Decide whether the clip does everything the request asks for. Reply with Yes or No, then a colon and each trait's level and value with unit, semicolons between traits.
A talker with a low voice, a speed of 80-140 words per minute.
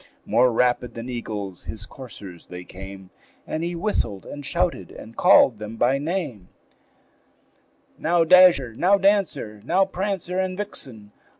Yes: low, 130 Hz; slow, 135 wpm